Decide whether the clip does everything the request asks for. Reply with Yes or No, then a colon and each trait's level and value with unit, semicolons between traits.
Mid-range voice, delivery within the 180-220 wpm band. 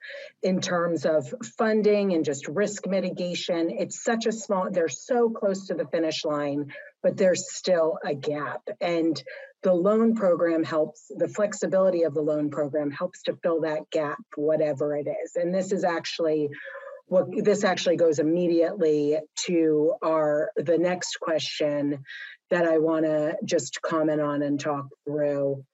No: medium, 165 Hz; average, 155 wpm